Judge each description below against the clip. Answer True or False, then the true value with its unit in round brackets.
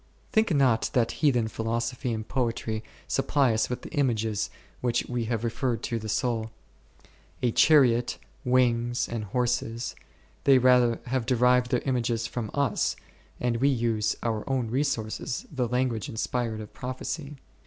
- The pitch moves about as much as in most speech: False (2.0 semitones)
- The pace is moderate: True (145 wpm)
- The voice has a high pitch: False (120 Hz)